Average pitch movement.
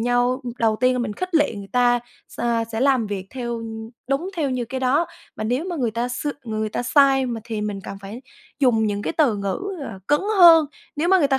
Yes: average, 4.0 semitones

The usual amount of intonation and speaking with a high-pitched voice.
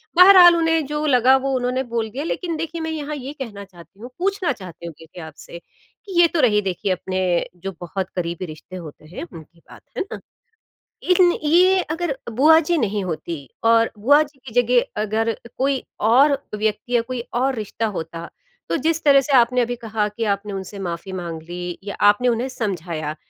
No: wide, 7.8 semitones; high, 230 Hz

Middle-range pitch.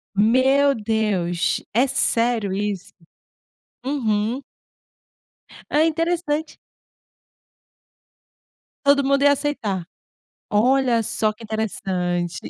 No: high, 230 Hz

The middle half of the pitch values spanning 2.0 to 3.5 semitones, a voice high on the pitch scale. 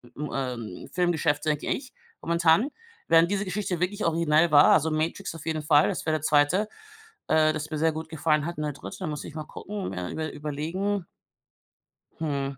No: narrow, 2.4 semitones; medium, 160 Hz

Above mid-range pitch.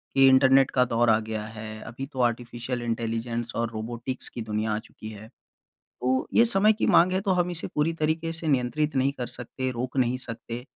No: low, 125 Hz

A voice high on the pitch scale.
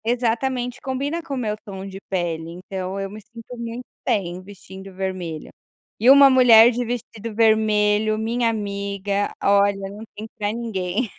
Yes: high, 215 Hz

